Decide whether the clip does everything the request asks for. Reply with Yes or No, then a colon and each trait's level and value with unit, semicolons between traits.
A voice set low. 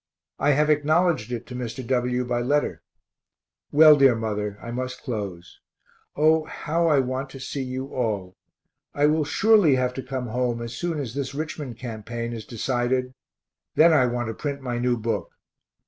Yes: low, 130 Hz